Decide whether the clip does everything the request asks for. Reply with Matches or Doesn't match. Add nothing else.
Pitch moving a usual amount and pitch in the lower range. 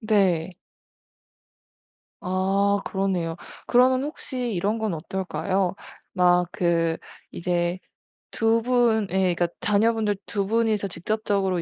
Doesn't match